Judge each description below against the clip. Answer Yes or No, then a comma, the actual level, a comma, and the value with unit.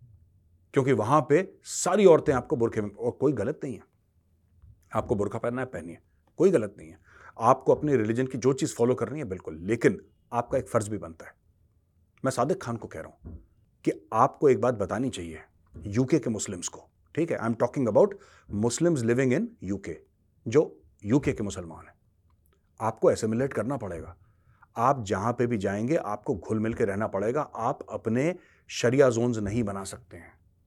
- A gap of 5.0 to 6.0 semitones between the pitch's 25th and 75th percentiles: Yes, average, 5.3 semitones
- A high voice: No, low, 110 Hz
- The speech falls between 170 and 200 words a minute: Yes, average, 180 wpm